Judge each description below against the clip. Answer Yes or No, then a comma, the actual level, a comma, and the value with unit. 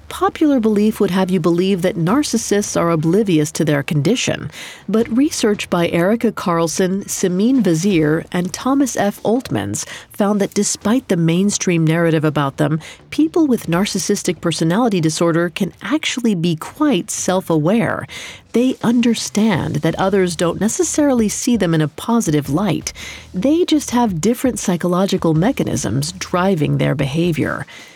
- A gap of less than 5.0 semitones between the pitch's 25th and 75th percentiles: No, wide, 5.4 semitones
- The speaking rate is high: No, slow, 135 wpm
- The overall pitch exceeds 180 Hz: Yes, high, 190 Hz